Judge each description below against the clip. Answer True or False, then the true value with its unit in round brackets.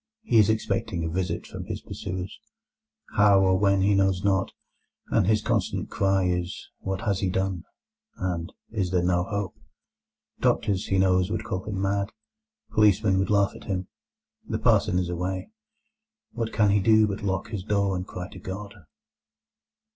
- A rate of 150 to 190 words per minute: True (160 wpm)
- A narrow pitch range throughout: True (1.7 semitones)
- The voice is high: False (95 Hz)